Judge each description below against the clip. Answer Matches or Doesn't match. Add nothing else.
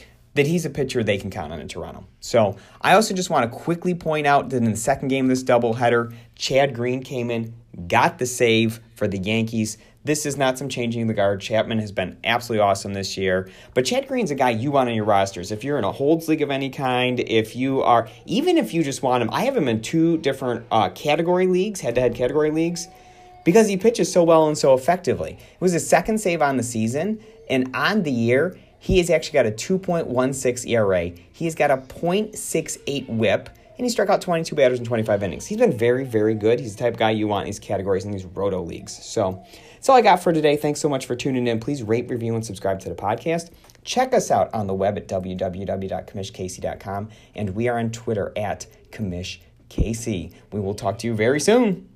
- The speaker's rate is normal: Doesn't match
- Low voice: Matches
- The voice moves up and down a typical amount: Doesn't match